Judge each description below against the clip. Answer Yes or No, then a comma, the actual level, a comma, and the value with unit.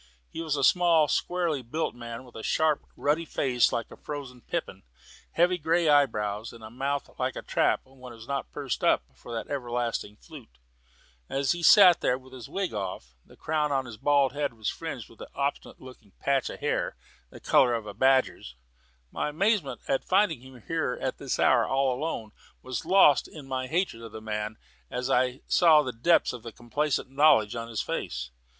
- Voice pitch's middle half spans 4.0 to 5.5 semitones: Yes, average, 4.4 semitones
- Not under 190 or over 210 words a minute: Yes, average, 195 wpm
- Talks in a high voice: No, low, 130 Hz